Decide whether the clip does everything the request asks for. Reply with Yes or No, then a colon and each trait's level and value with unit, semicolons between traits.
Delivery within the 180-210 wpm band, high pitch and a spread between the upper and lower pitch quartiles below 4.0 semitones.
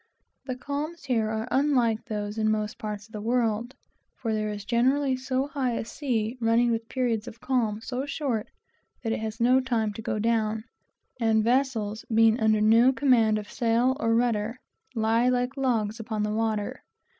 Yes: average, 185 wpm; high, 230 Hz; average, 2.7 semitones